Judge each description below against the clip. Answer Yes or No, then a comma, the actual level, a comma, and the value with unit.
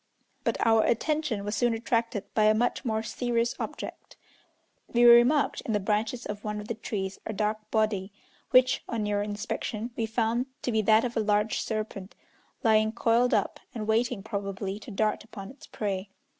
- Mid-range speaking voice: No, high, 220 Hz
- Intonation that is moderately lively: No, narrow, 2.1 semitones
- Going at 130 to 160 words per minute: No, average, 180 wpm